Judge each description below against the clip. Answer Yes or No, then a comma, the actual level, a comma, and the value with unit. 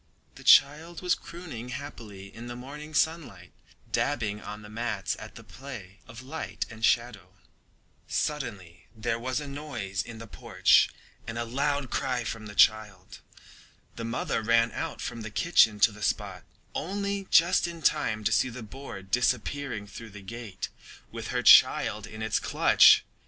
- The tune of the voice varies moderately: Yes, average, 5.0 semitones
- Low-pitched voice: Yes, low, 115 Hz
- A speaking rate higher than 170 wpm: No, average, 160 wpm